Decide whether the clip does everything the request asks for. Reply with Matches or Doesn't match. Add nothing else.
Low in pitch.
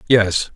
Matches